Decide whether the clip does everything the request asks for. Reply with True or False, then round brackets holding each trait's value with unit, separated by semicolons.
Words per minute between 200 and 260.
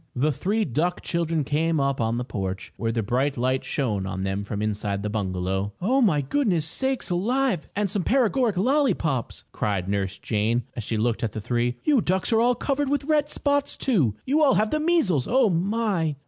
True (205 wpm)